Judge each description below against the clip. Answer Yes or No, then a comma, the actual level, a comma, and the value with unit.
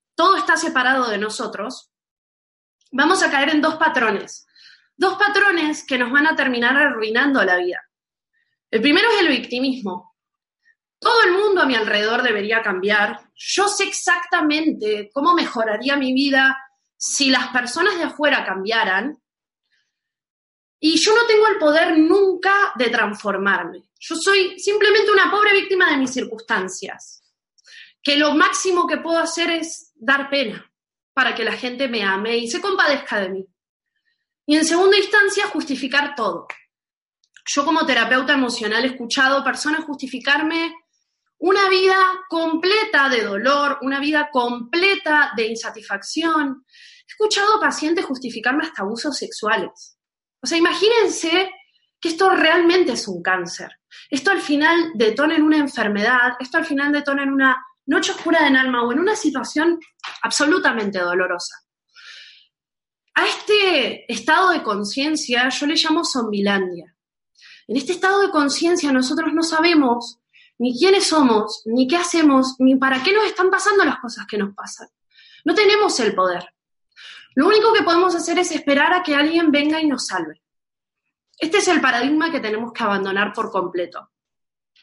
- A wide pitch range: Yes, wide, 6.5 semitones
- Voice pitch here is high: Yes, very high, 290 Hz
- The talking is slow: No, average, 150 wpm